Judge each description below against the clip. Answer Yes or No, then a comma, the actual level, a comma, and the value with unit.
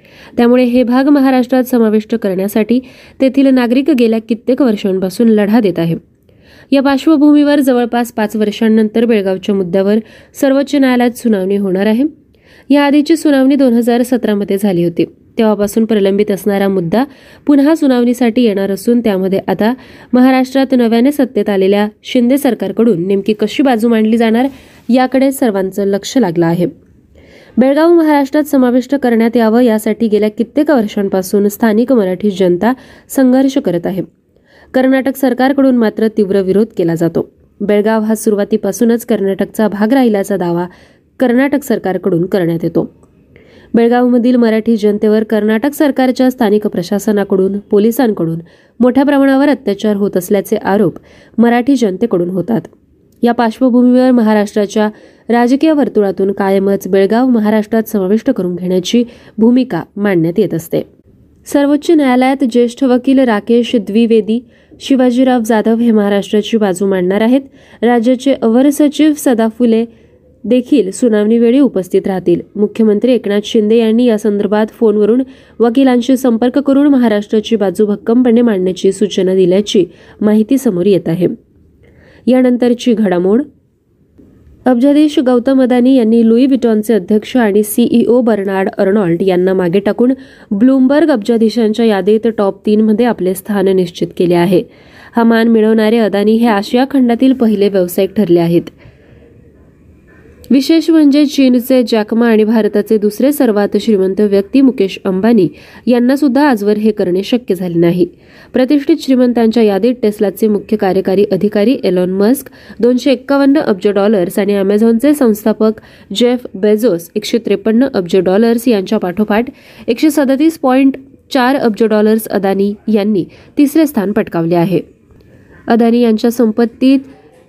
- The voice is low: No, high, 225 Hz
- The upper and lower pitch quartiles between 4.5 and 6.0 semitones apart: No, average, 3.8 semitones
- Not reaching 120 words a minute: No, average, 125 wpm